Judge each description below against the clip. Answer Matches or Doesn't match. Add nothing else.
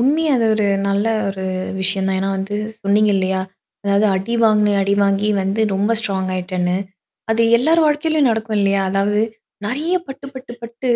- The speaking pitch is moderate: Doesn't match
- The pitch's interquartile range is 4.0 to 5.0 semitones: Doesn't match